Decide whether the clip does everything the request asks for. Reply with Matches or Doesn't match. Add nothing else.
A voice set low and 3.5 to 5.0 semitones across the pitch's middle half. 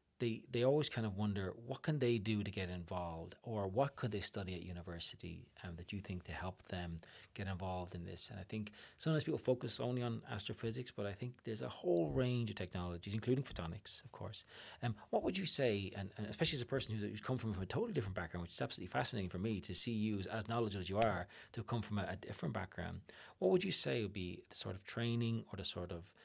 Matches